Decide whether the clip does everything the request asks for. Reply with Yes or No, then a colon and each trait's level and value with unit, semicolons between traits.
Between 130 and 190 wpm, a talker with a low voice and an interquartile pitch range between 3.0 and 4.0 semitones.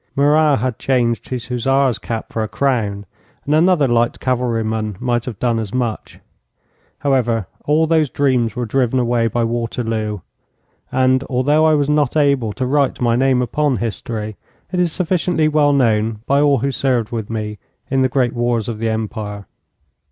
Yes: average, 175 wpm; low, 125 Hz; average, 3.6 semitones